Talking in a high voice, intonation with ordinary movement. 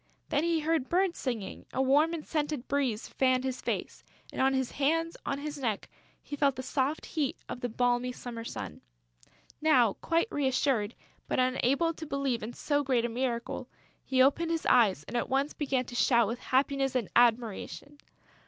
Yes: very high, 265 Hz; average, 3.2 semitones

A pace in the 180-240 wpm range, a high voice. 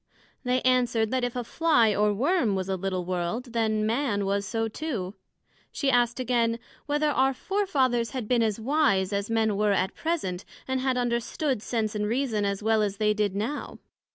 Yes: average, 190 wpm; high, 230 Hz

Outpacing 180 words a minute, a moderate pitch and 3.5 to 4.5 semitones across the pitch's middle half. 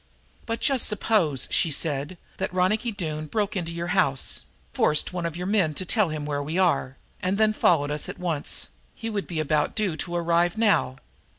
No: average, 195 wpm; medium, 175 Hz; average, 5.0 semitones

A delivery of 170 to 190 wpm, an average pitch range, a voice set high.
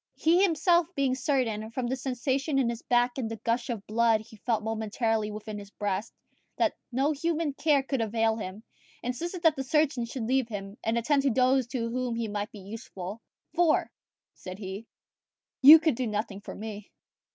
Yes: average, 185 wpm; average, 3.9 semitones; high, 235 Hz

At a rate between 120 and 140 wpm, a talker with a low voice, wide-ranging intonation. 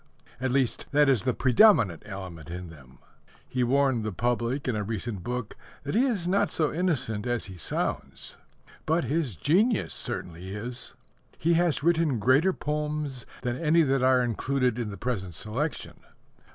No: average, 165 wpm; low, 125 Hz; wide, 5.9 semitones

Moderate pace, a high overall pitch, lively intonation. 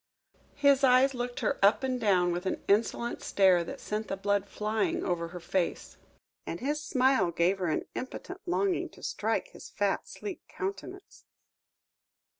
Yes: average, 160 wpm; high, 215 Hz; wide, 6.3 semitones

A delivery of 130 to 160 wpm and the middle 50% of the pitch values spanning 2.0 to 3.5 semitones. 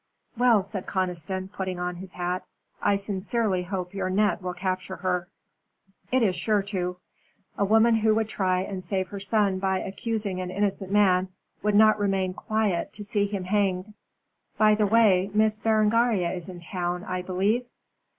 No: average, 170 wpm; narrow, 2.4 semitones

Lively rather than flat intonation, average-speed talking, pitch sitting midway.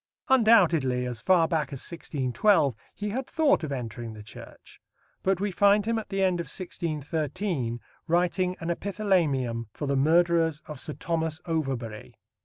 Yes: wide, 5.8 semitones; average, 155 wpm; medium, 165 Hz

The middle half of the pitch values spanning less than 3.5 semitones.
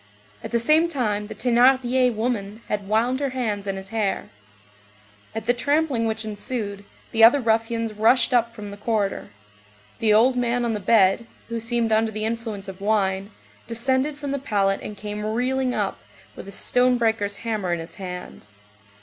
Yes: average, 3.1 semitones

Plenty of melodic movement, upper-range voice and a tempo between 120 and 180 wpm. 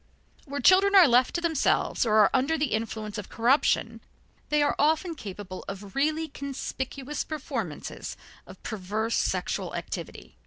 Yes: wide, 5.9 semitones; very high, 265 Hz; average, 145 wpm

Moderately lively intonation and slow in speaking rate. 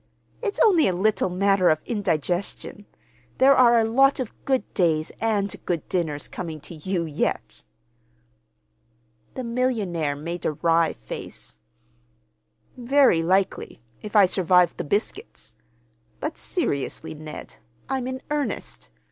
No: wide, 6.8 semitones; slow, 120 wpm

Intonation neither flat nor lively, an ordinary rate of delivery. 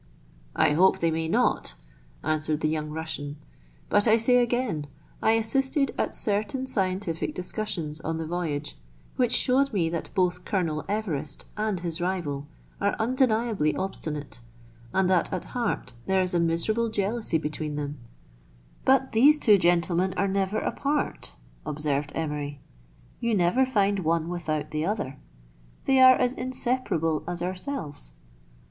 No: wide, 6.2 semitones; average, 145 wpm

